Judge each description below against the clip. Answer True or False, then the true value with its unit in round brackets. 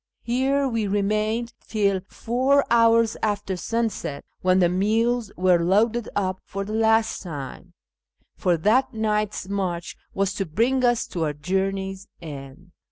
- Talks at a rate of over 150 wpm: False (140 wpm)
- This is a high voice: True (205 Hz)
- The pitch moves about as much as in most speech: True (3.8 semitones)